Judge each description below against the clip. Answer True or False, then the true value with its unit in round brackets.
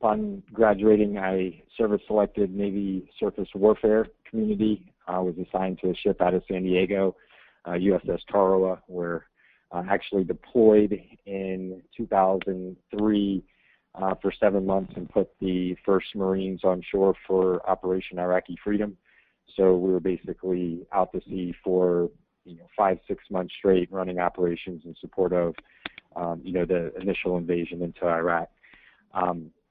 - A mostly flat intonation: True (1.7 semitones)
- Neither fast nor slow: True (145 wpm)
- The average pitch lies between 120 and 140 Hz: False (95 Hz)